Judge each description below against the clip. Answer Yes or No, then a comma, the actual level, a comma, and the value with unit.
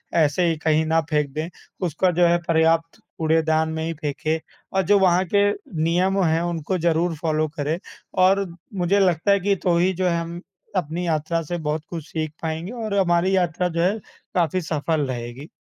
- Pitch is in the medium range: Yes, medium, 165 Hz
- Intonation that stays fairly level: Yes, narrow, 2.3 semitones